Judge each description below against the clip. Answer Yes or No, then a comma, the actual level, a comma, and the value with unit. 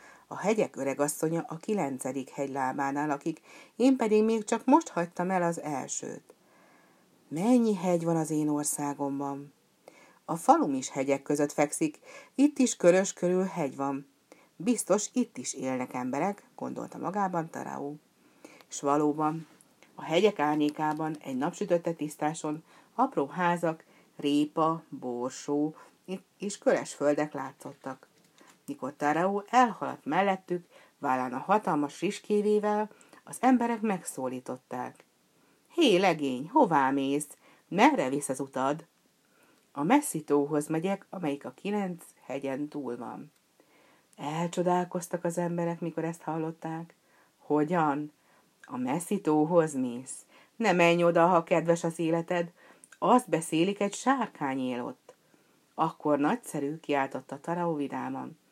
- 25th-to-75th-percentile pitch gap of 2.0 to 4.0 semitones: No, average, 4.7 semitones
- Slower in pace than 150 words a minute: Yes, average, 120 wpm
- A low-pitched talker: No, medium, 165 Hz